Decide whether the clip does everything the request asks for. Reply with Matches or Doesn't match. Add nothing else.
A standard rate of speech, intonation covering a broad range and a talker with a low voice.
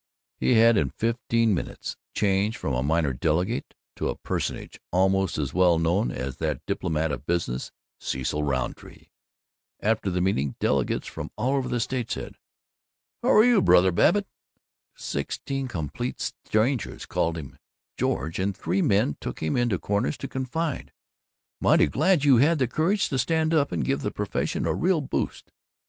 Matches